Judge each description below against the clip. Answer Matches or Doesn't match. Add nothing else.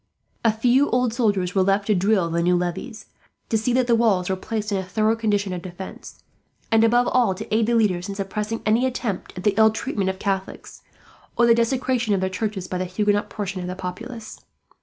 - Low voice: Doesn't match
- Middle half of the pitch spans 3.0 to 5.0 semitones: Matches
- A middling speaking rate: Doesn't match